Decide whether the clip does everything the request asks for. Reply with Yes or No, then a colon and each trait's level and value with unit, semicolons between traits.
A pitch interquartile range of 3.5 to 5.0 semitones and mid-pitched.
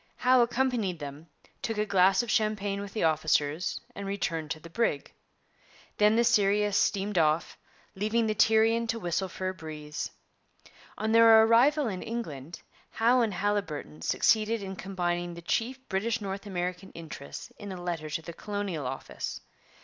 No: average, 4.7 semitones; high, 195 Hz